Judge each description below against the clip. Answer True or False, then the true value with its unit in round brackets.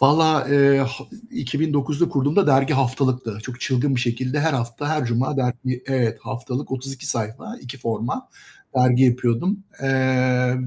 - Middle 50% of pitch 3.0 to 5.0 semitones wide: False (2.4 semitones)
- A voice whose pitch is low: True (130 Hz)